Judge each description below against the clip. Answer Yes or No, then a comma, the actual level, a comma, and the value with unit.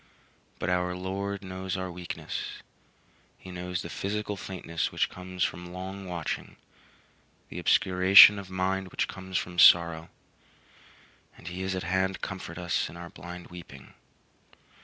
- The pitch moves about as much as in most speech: No, narrow, 1.3 semitones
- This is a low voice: Yes, very low, 90 Hz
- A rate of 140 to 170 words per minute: Yes, average, 145 wpm